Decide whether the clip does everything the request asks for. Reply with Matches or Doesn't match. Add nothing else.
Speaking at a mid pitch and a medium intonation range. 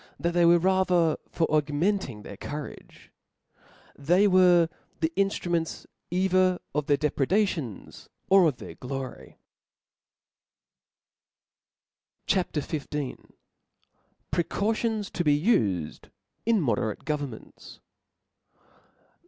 Matches